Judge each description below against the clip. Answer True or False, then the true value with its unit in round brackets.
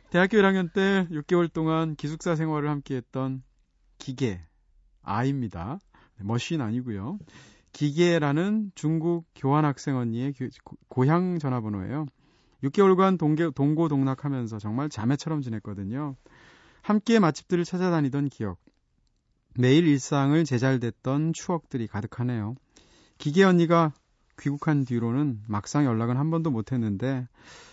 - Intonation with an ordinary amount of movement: True (4.9 semitones)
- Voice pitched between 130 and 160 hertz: True (140 Hz)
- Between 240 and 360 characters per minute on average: True (280 characters per minute)